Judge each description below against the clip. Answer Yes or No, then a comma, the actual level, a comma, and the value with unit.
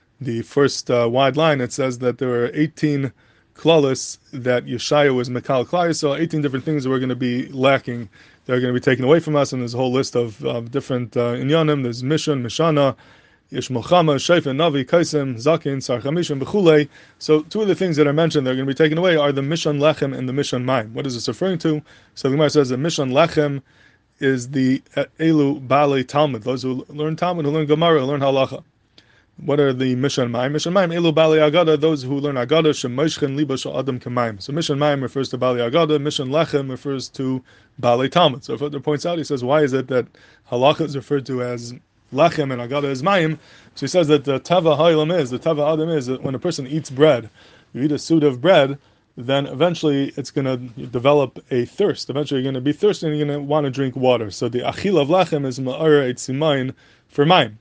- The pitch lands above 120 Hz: Yes, medium, 140 Hz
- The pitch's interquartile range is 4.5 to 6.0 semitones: No, average, 3.2 semitones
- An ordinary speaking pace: No, fast, 220 wpm